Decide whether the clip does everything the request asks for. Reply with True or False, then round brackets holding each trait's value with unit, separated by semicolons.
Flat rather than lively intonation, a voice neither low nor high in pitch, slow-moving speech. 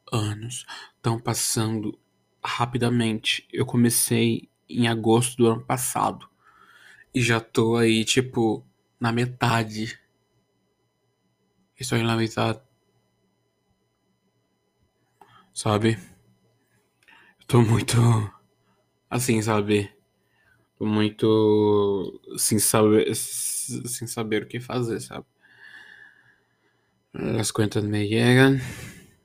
False (2.0 semitones; 115 Hz; 85 wpm)